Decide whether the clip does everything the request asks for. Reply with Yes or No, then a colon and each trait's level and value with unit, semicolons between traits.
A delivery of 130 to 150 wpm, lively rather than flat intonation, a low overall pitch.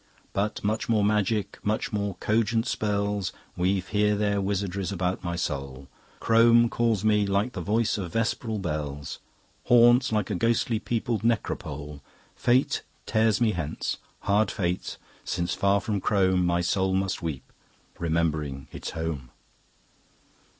No: slow, 135 wpm; average, 3.8 semitones; low, 100 Hz